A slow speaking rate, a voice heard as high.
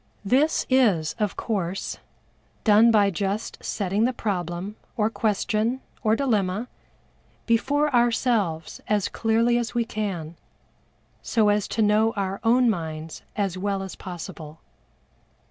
Yes: slow, 125 wpm; high, 210 Hz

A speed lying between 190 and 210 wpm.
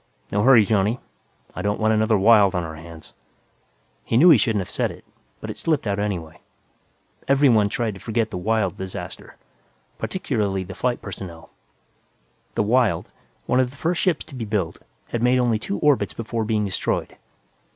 No: average, 175 wpm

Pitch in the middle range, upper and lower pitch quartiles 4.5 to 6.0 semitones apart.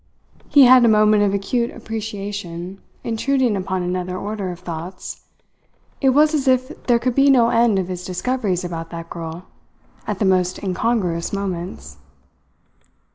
No: high, 200 Hz; average, 4.8 semitones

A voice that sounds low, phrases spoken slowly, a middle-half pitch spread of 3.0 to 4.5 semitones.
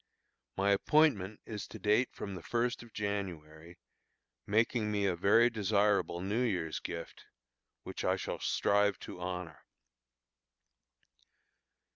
Yes: low, 100 Hz; slow, 120 wpm; average, 3.3 semitones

